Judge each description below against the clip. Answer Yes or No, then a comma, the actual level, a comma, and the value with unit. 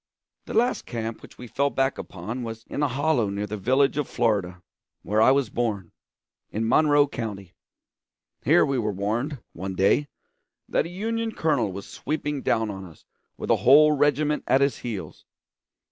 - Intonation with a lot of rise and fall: Yes, wide, 5.8 semitones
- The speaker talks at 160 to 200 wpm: Yes, average, 175 wpm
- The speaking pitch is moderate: No, low, 120 Hz